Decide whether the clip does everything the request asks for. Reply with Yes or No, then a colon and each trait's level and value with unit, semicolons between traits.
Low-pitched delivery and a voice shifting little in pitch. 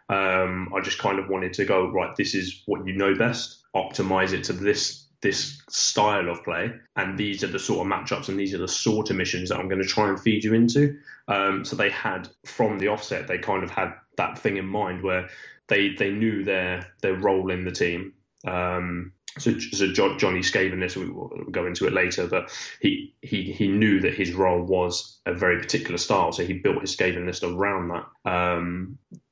Yes: very low, 95 Hz; narrow, 2.3 semitones